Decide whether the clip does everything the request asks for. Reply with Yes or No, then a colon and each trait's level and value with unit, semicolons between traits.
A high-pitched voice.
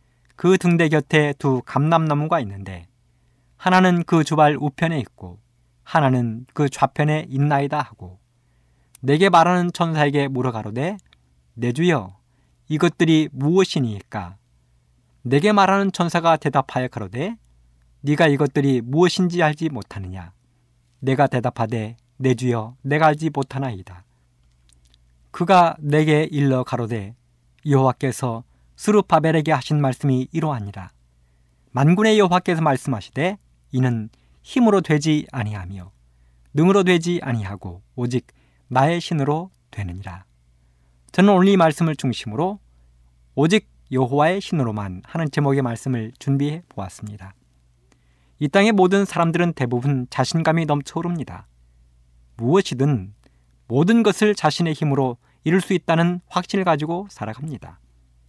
No: low, 135 Hz